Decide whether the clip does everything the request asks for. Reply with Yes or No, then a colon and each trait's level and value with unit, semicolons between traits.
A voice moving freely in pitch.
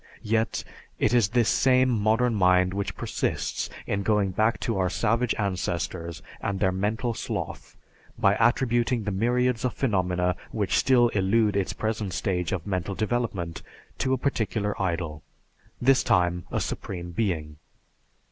No: average, 4.1 semitones